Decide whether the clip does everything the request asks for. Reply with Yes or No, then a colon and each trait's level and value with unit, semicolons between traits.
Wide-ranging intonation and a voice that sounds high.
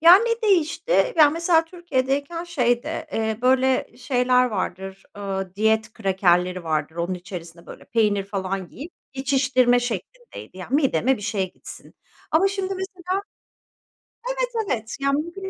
Yes: wide, 9.0 semitones; very high, 250 Hz